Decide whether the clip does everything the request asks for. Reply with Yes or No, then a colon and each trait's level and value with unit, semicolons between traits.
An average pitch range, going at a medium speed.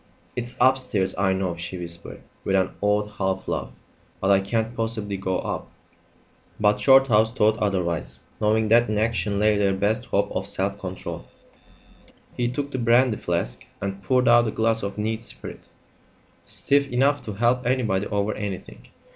Yes: average, 3.5 semitones; average, 165 wpm